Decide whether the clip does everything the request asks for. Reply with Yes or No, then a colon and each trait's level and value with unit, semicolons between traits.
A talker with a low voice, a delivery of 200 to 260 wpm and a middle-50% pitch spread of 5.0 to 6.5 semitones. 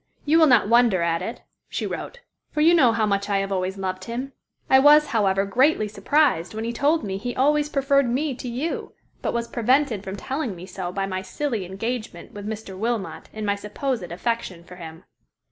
No: high, 225 Hz; fast, 205 wpm; wide, 5.6 semitones